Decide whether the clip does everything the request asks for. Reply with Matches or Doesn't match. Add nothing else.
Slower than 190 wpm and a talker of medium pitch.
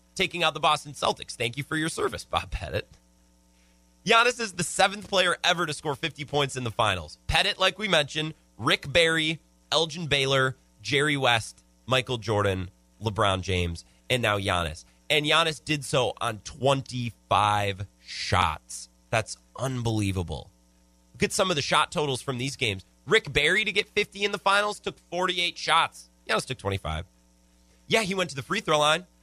Doesn't match